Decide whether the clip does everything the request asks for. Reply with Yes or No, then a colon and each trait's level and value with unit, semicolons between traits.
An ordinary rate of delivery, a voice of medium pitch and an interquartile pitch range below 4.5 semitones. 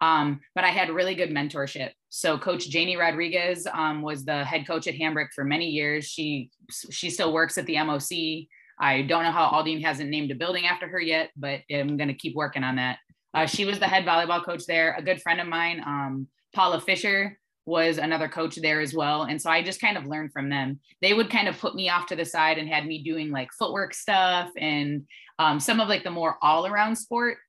No: fast, 230 wpm; medium, 160 Hz; average, 2.9 semitones